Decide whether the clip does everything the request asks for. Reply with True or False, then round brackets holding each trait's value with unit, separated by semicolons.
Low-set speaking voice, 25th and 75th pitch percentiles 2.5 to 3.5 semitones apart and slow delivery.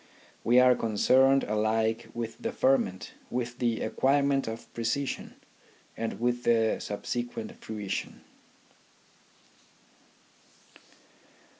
True (120 Hz; 3.0 semitones; 90 wpm)